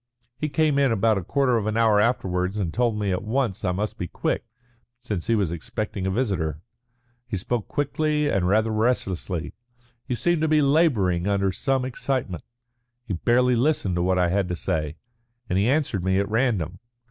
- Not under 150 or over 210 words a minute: Yes, average, 195 wpm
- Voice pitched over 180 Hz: No, low, 105 Hz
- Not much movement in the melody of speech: No, wide, 5.5 semitones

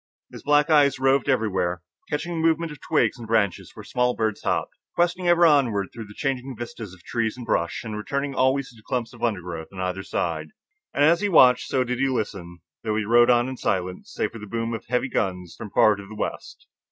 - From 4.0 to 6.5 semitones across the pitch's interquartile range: Yes, average, 5.2 semitones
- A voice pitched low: Yes, low, 120 Hz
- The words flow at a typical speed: No, fast, 225 wpm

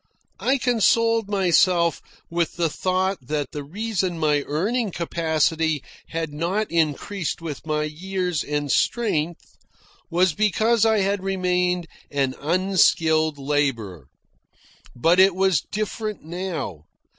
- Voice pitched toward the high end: No, medium, 175 Hz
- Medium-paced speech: No, slow, 115 wpm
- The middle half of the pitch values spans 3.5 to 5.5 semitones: Yes, average, 4.2 semitones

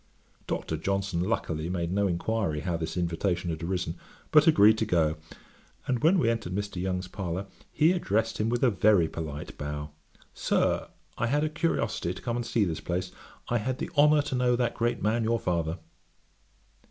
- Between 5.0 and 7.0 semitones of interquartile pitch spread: Yes, wide, 5.5 semitones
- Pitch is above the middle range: No, low, 100 Hz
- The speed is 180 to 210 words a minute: Yes, average, 185 wpm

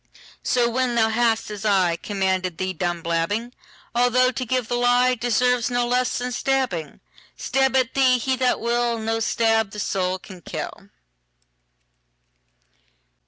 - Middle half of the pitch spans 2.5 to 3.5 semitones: No, average, 4.1 semitones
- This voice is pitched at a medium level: No, high, 235 Hz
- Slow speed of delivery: Yes, slow, 120 wpm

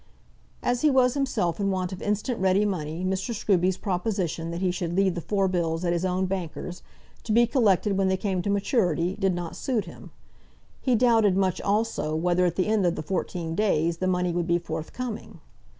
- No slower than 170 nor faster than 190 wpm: No, average, 200 wpm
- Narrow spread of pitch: No, average, 3.2 semitones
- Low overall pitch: No, medium, 185 Hz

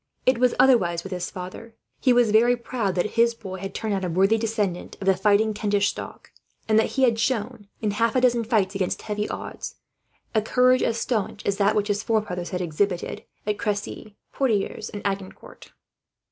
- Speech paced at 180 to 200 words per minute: Yes, average, 195 wpm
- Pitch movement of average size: Yes, average, 3.0 semitones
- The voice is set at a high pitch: Yes, high, 210 Hz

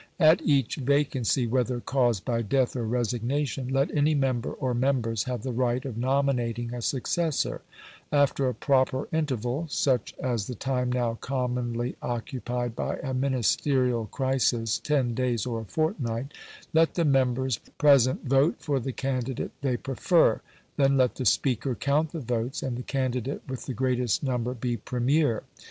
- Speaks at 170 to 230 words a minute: No, average, 155 wpm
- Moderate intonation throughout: No, narrow, 2.2 semitones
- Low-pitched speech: Yes, low, 130 Hz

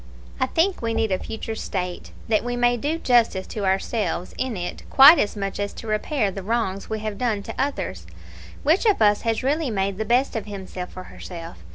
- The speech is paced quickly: Yes, fast, 215 wpm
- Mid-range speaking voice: No, high, 215 Hz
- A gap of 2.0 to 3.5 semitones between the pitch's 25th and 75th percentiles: No, average, 4.0 semitones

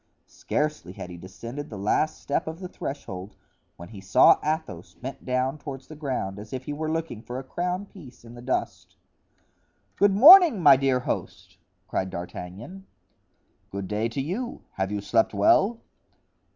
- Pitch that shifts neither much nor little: No, wide, 7.7 semitones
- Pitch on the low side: Yes, low, 130 Hz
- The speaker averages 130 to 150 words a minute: No, average, 165 wpm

